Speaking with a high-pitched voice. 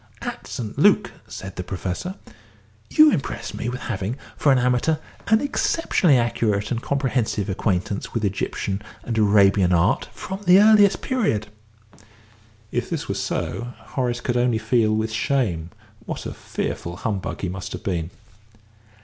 No: low, 115 Hz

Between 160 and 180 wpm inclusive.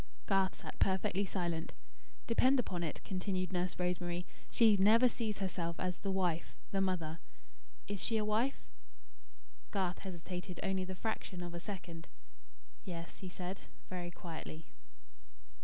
No: average, 140 wpm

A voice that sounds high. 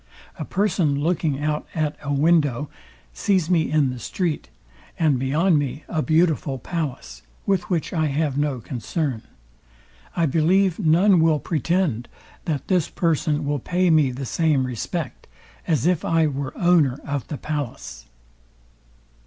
No: medium, 155 Hz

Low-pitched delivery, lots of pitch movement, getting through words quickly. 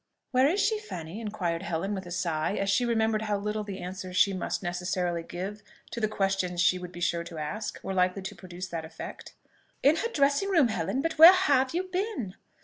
No: high, 195 Hz; wide, 6.3 semitones; fast, 215 wpm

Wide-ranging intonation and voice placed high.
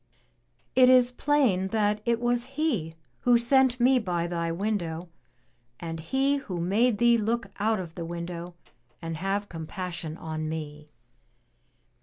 Yes: wide, 6.3 semitones; high, 200 Hz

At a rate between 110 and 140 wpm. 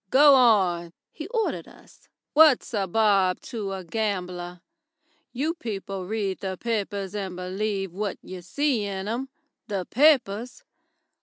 Yes: slow, 135 wpm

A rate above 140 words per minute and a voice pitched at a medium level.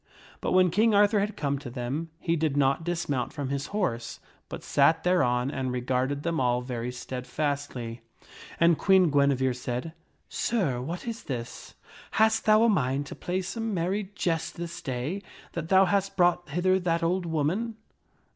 Yes: average, 170 wpm; medium, 160 Hz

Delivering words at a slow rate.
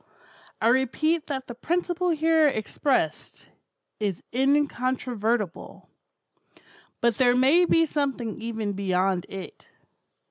Yes: slow, 100 wpm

